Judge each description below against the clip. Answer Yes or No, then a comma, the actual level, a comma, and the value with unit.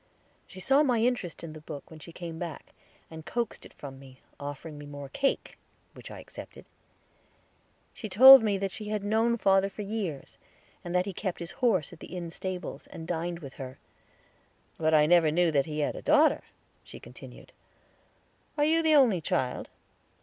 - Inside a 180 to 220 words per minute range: Yes, average, 185 wpm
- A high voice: No, medium, 175 Hz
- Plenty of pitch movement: Yes, wide, 6.0 semitones